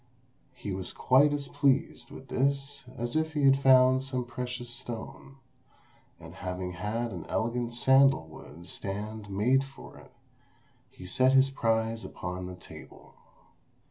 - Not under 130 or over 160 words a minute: Yes, average, 140 wpm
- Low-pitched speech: Yes, low, 120 Hz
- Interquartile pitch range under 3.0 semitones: No, average, 4.6 semitones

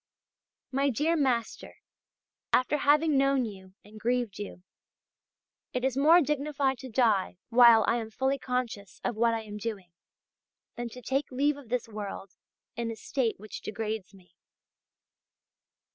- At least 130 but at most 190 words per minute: Yes, average, 145 wpm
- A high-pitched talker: Yes, high, 240 Hz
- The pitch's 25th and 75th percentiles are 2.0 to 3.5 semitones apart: No, average, 3.9 semitones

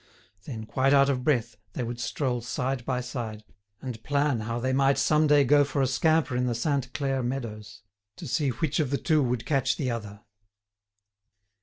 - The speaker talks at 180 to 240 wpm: Yes, average, 190 wpm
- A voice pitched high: No, low, 130 Hz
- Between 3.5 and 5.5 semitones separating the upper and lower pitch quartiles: No, average, 2.9 semitones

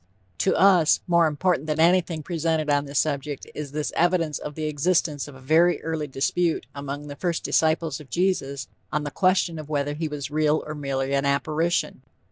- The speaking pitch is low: No, medium, 155 Hz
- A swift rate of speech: No, average, 190 wpm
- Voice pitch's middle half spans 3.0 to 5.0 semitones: No, narrow, 2.5 semitones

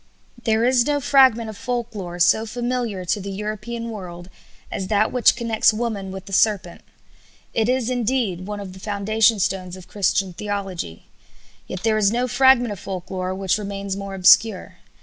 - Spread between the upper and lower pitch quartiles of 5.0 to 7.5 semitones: No, average, 3.4 semitones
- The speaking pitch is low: No, high, 210 Hz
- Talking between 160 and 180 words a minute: Yes, average, 175 wpm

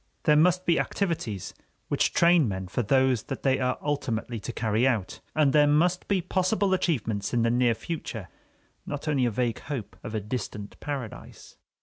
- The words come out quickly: No, average, 180 wpm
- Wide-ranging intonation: Yes, wide, 5.7 semitones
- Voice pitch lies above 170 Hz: No, low, 130 Hz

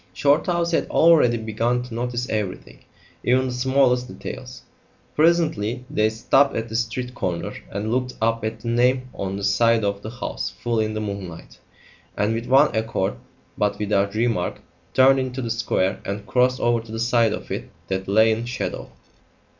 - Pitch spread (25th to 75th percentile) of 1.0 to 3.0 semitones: Yes, average, 2.7 semitones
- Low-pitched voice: Yes, low, 115 Hz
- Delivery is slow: No, average, 175 wpm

